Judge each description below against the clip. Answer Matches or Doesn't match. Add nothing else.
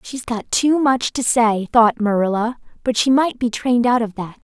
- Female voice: Matches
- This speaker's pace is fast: Matches